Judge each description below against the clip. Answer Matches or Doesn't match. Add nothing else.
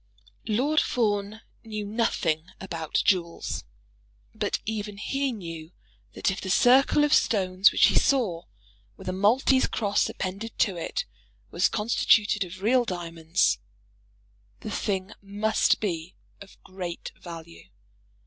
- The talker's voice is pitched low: Doesn't match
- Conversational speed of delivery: Doesn't match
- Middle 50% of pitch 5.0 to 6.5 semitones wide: Doesn't match